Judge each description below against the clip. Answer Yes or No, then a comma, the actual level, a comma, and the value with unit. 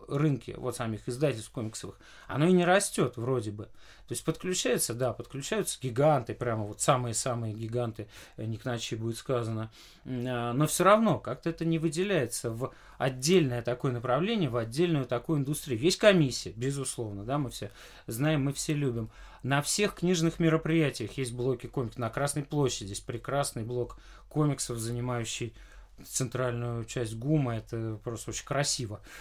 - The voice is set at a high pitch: No, low, 125 Hz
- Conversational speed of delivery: Yes, average, 150 wpm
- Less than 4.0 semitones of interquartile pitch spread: No, average, 4.6 semitones